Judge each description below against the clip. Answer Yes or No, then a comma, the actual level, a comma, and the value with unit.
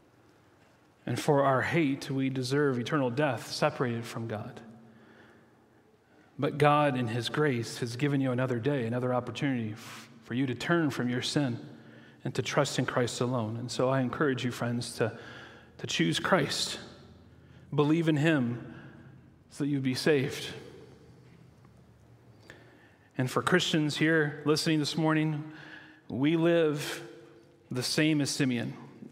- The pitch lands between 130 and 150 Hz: Yes, low, 135 Hz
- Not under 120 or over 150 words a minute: Yes, average, 140 wpm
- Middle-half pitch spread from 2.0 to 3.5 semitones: No, average, 4.1 semitones